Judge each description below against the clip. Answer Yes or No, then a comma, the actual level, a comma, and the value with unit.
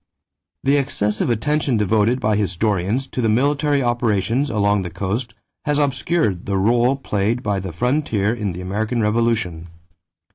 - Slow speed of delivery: No, average, 150 wpm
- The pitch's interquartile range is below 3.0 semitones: No, average, 4.2 semitones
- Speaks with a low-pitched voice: Yes, low, 110 Hz